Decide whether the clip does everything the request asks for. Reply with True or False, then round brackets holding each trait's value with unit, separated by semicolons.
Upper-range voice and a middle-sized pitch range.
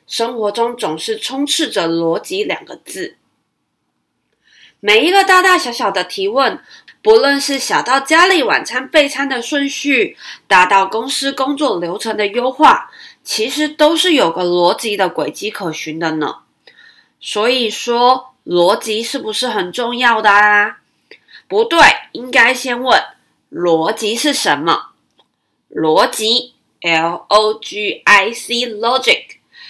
False (245 Hz; 6.3 semitones)